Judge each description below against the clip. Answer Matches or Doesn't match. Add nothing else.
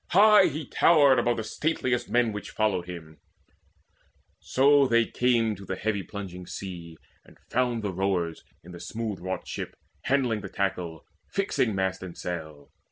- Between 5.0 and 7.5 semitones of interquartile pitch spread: Matches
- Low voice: Matches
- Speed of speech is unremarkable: Matches